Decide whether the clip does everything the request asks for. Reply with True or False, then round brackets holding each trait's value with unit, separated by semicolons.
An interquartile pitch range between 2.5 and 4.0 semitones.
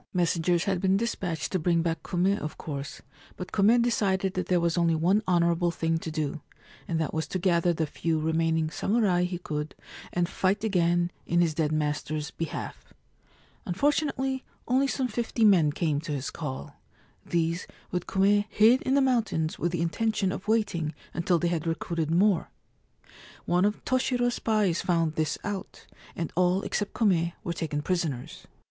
True (3.7 semitones)